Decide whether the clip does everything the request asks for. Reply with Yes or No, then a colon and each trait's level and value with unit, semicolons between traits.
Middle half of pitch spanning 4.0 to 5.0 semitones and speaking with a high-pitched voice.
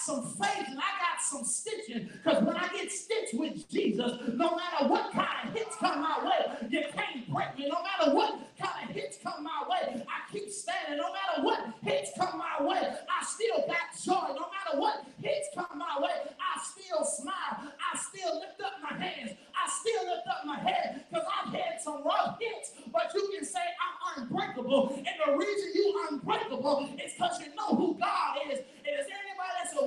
Yes: average, 4.3 semitones; very high, 340 Hz